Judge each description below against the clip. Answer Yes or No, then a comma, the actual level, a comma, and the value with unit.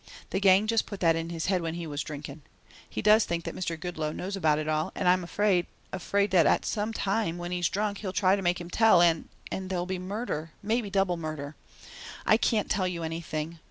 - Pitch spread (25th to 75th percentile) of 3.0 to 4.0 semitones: Yes, average, 3.4 semitones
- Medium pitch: Yes, medium, 180 Hz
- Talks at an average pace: No, fast, 225 wpm